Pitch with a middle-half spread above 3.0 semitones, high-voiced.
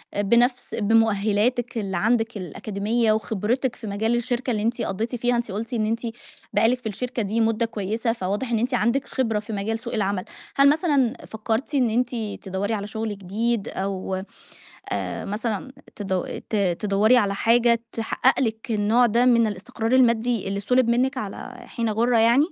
No: average, 2.7 semitones; high, 225 Hz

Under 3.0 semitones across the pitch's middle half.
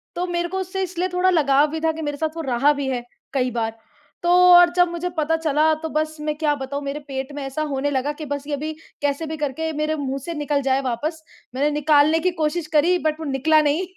Yes: narrow, 2.4 semitones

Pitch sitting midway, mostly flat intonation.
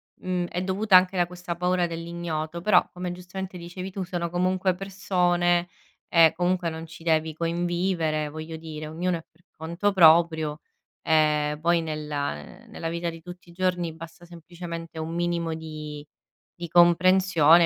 Yes: medium, 170 Hz; narrow, 1.9 semitones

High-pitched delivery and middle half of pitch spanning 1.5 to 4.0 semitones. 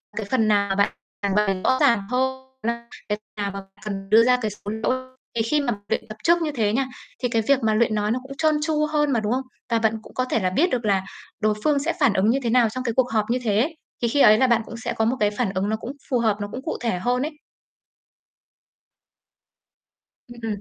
Yes: high, 230 Hz; average, 3.6 semitones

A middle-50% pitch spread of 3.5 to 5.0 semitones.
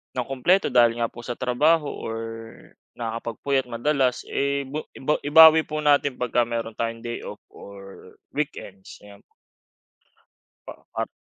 Yes: average, 3.8 semitones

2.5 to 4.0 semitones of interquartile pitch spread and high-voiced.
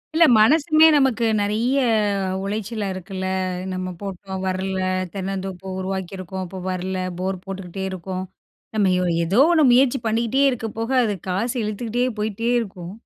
Yes: average, 3.6 semitones; high, 195 Hz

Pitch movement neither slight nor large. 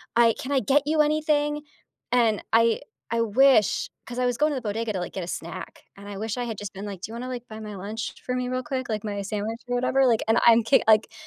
Yes: average, 3.2 semitones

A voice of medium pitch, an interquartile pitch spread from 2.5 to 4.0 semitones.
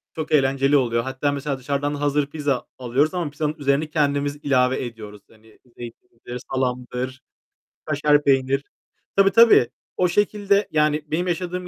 Yes: medium, 145 Hz; average, 3.0 semitones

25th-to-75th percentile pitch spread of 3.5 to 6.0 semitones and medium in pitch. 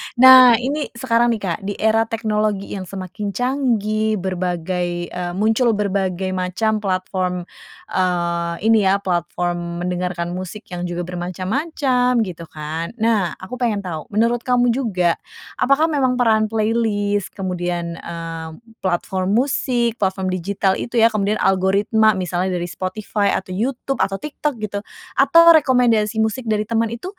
No: average, 4.2 semitones; high, 205 Hz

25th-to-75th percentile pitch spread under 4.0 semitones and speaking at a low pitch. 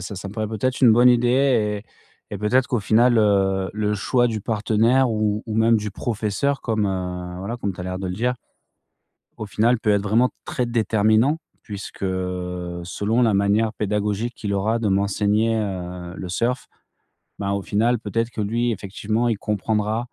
Yes: average, 2.8 semitones; low, 105 Hz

